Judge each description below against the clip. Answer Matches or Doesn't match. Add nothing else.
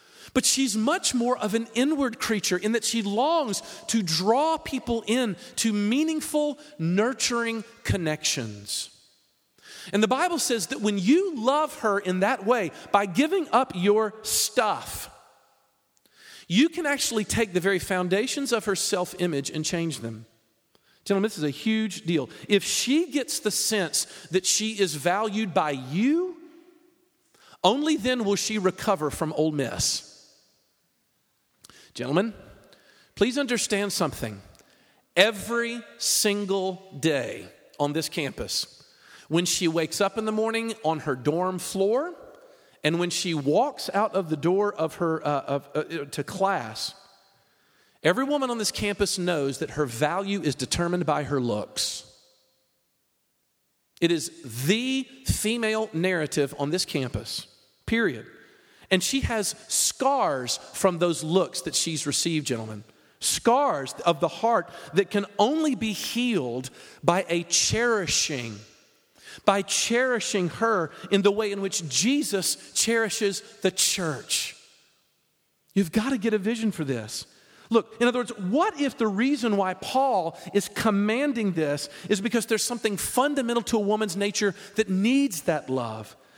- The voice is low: Doesn't match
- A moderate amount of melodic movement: Doesn't match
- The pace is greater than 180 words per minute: Doesn't match